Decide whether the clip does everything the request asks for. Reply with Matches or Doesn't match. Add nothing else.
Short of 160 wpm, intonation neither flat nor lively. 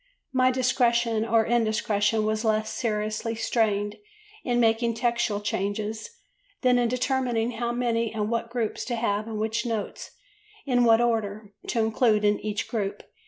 Doesn't match